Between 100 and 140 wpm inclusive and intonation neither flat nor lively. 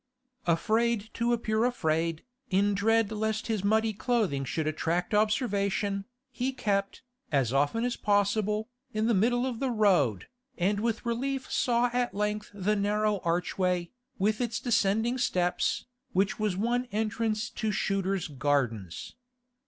Yes: slow, 135 wpm; average, 3.5 semitones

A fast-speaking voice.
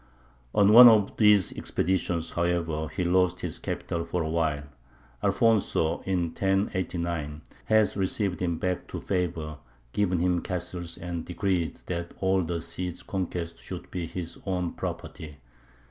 No: average, 140 wpm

